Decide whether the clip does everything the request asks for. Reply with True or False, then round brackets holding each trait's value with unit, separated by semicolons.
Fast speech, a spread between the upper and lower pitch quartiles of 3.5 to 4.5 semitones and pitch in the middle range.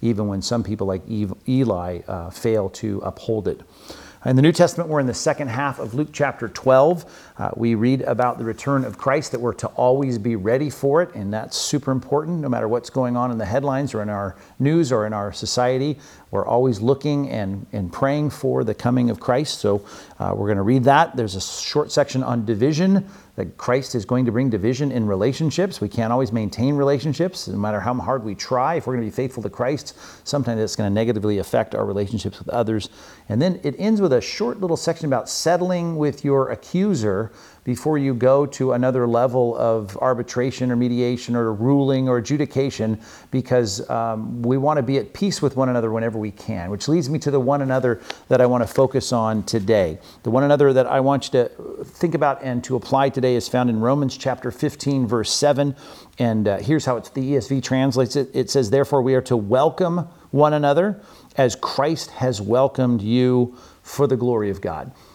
False (210 wpm; 3.8 semitones; 125 Hz)